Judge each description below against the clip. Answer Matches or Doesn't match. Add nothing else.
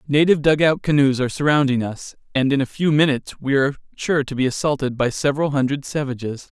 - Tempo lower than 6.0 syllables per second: Doesn't match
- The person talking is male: Matches